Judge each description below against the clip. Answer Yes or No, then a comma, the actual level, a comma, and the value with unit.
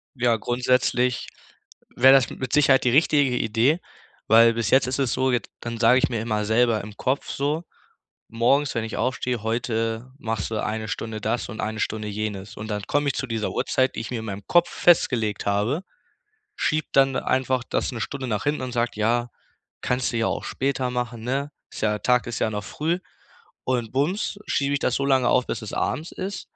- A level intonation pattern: No, average, 3.1 semitones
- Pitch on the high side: No, low, 120 Hz